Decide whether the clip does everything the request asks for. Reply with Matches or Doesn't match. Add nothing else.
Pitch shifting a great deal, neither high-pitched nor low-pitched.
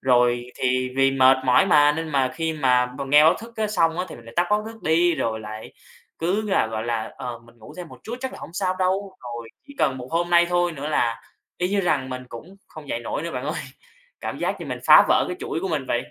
Matches